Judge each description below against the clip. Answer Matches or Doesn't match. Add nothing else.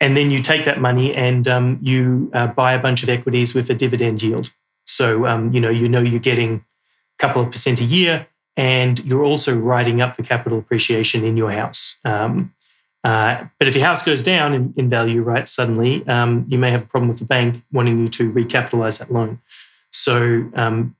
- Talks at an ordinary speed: Doesn't match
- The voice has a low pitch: Matches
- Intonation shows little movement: Matches